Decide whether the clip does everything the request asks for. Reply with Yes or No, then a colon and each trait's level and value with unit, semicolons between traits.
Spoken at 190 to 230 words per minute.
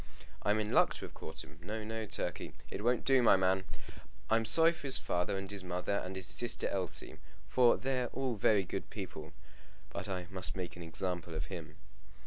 Yes: average, 200 wpm